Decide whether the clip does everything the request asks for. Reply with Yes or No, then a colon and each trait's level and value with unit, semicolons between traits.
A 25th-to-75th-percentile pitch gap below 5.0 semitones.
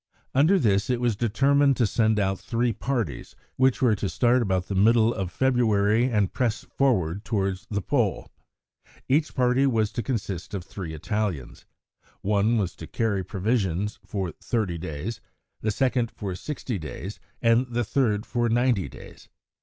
Yes: average, 4.0 semitones